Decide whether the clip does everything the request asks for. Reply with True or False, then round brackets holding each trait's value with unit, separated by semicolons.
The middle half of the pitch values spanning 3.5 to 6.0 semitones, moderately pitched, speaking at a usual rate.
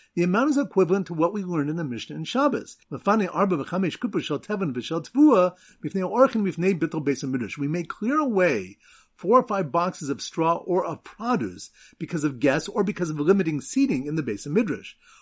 True (4.5 semitones; 180 Hz; 155 wpm)